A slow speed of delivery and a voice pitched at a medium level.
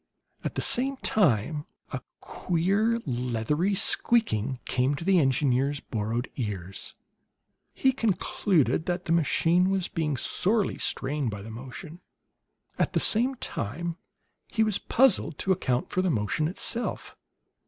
Yes: slow, 130 wpm; medium, 160 Hz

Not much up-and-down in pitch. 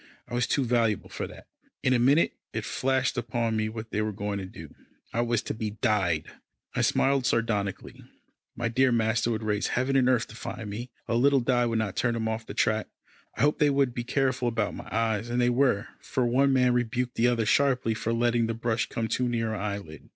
Yes: narrow, 2.3 semitones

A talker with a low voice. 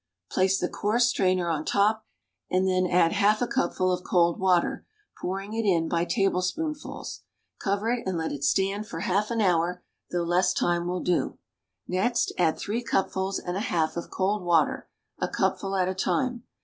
No: medium, 185 Hz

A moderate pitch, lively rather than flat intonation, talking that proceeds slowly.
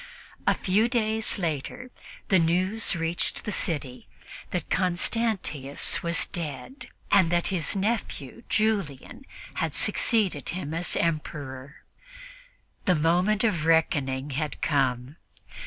Yes: medium, 170 Hz; wide, 6.0 semitones; slow, 110 wpm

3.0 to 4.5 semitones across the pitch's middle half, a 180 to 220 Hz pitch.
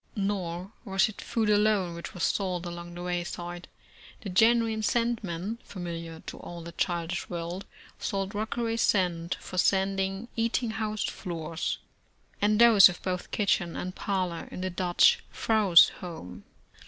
Yes: average, 3.5 semitones; medium, 185 Hz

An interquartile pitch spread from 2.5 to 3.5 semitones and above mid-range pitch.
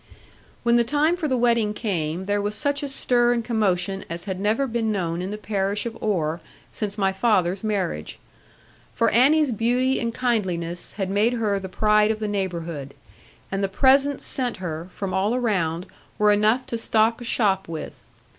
No: average, 3.9 semitones; high, 210 Hz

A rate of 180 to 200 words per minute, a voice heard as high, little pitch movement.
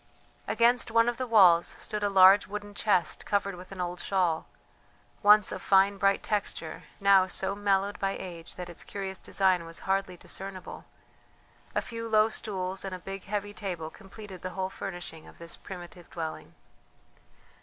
No: average, 165 wpm; high, 195 Hz; narrow, 2.1 semitones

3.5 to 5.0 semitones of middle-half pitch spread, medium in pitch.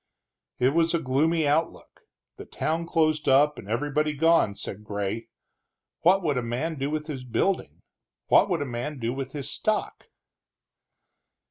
Yes: average, 4.3 semitones; medium, 150 Hz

